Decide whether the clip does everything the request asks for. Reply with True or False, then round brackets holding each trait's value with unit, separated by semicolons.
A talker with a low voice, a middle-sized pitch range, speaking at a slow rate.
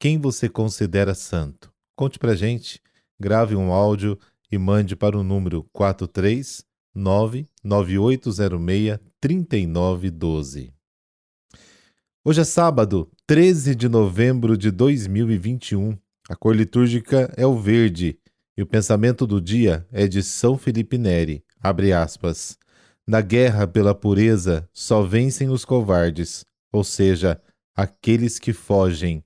True (105 Hz; 3.8 semitones; 115 wpm)